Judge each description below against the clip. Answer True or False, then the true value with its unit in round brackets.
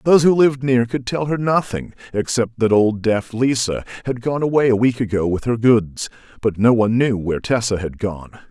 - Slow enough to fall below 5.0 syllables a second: False (5.4 syllables/s)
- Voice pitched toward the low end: True (120 Hz)